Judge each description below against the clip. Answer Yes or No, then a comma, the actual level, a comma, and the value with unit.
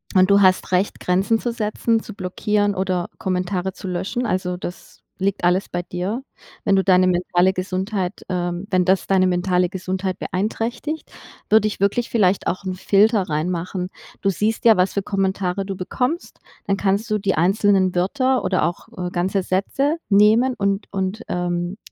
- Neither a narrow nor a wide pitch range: No, narrow, 2.2 semitones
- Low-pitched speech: No, high, 190 Hz